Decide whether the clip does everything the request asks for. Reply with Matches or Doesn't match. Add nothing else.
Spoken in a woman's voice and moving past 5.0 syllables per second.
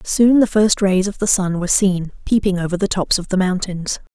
Matches